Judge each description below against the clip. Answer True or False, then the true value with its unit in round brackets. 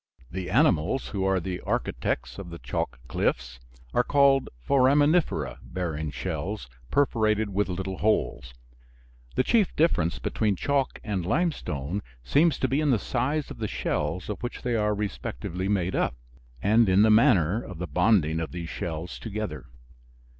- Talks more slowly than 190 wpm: True (155 wpm)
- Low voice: True (100 Hz)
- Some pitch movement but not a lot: False (6.6 semitones)